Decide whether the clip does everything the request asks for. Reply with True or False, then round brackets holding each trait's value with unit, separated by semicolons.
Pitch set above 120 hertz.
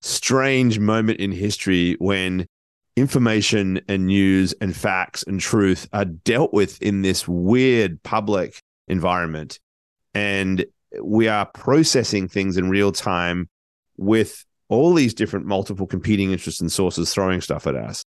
False (100 Hz)